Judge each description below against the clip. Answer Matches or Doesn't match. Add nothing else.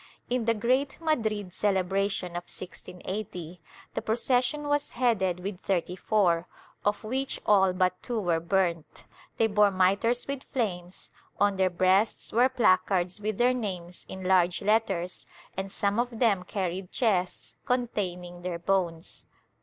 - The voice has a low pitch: Doesn't match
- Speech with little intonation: Doesn't match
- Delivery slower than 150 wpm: Matches